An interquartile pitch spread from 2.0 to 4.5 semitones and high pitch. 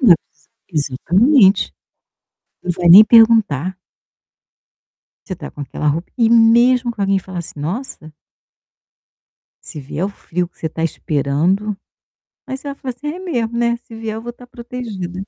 No: wide, 5.6 semitones; high, 205 Hz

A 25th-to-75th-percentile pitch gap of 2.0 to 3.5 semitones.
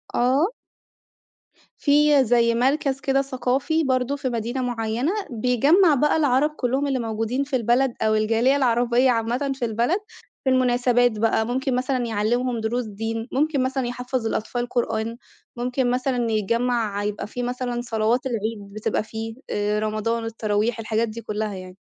Yes: average, 2.7 semitones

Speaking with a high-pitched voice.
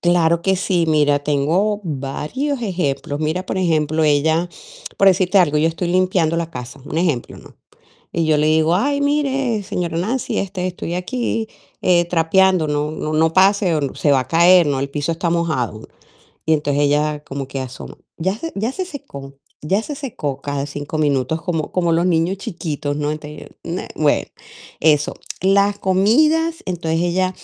No: medium, 165 Hz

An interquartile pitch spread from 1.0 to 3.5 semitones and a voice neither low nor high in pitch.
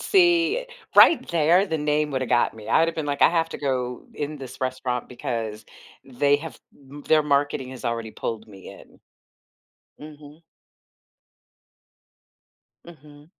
No: average, 3.9 semitones; medium, 145 Hz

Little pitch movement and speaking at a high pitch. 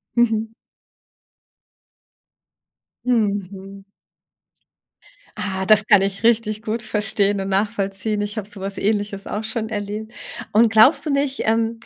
Yes: narrow, 2.0 semitones; high, 215 Hz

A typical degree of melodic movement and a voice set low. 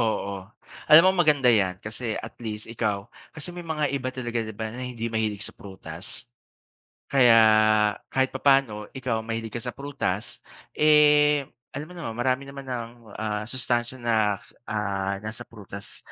Yes: average, 4.0 semitones; low, 120 Hz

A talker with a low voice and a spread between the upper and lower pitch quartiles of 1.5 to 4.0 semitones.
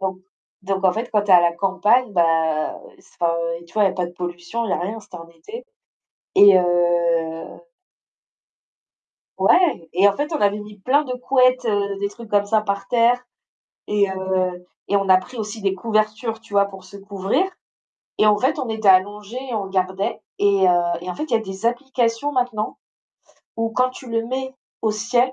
No: high, 205 Hz; average, 3.6 semitones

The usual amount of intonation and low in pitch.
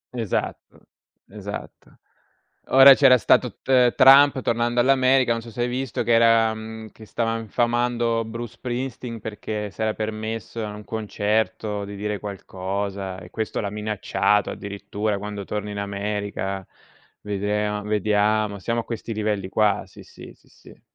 No: narrow, 2.2 semitones; low, 110 Hz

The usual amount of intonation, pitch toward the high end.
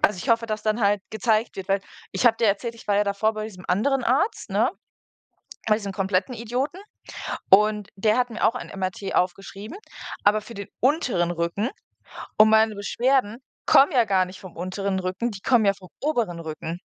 Yes: average, 3.2 semitones; high, 210 Hz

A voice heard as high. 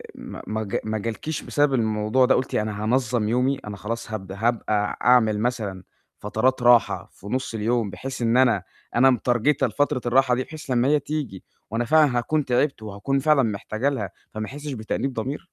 No: low, 120 Hz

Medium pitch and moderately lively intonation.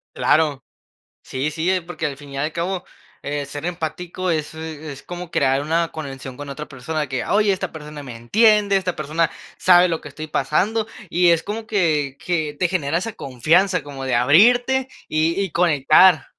Yes: medium, 160 Hz; average, 3.9 semitones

